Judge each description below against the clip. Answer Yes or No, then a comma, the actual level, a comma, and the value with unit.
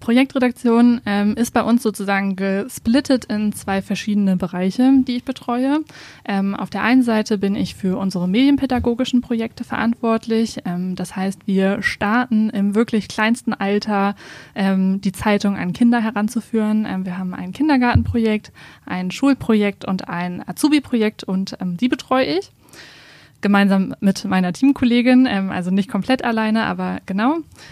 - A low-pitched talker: No, high, 215 Hz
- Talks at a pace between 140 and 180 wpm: Yes, average, 145 wpm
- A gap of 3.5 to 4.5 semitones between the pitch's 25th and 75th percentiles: Yes, average, 3.9 semitones